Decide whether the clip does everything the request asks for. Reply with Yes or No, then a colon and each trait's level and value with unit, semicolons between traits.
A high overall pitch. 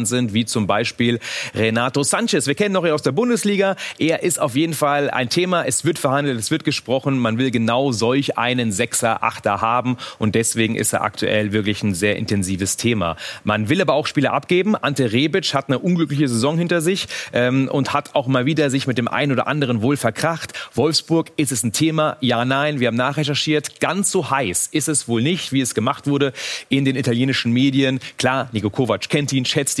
No: low, 135 Hz